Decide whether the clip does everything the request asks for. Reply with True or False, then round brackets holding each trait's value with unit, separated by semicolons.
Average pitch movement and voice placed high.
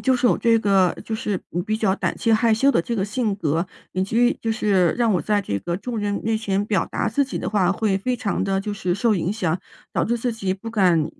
True (3.1 semitones; 205 Hz)